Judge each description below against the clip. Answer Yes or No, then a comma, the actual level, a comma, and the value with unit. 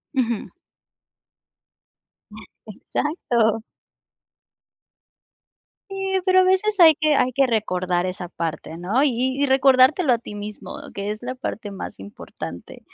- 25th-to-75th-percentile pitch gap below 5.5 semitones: No, wide, 6.5 semitones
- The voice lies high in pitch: Yes, high, 245 Hz